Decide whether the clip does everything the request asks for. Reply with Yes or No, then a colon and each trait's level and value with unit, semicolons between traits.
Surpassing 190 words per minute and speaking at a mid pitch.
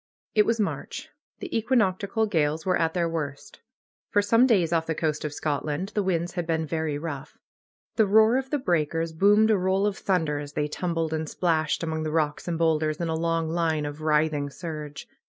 Yes: average, 200 wpm; medium, 165 Hz